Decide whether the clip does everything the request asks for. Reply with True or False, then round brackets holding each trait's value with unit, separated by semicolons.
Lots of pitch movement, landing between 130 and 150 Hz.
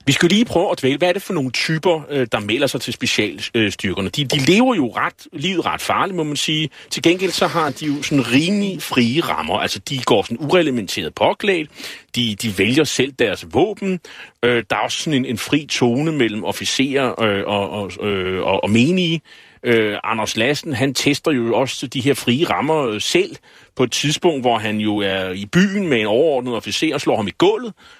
True (6.6 semitones; 140 Hz)